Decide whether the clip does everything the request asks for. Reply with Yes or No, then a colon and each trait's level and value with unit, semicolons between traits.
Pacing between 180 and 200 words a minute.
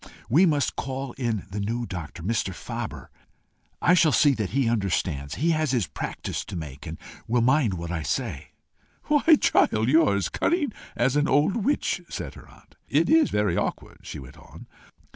Yes: average, 185 wpm